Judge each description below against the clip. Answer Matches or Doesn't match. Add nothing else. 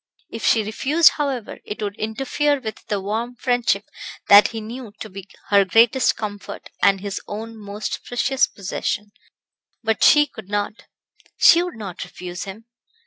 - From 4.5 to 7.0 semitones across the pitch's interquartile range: Doesn't match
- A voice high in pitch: Matches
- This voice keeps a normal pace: Matches